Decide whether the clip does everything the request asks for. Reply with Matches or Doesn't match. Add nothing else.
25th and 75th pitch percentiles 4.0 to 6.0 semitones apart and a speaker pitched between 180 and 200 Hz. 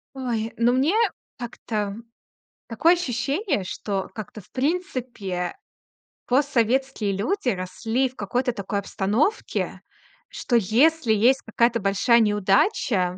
Doesn't match